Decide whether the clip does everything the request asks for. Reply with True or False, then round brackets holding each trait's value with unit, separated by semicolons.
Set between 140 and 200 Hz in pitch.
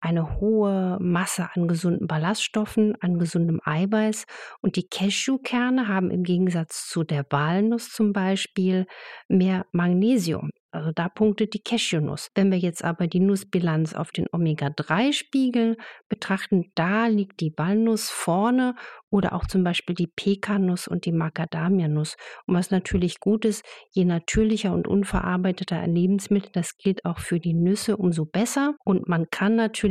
True (190 Hz)